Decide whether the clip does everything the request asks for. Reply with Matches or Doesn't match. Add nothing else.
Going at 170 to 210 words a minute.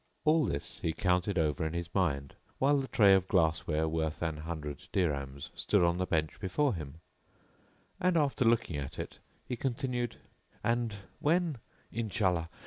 Doesn't match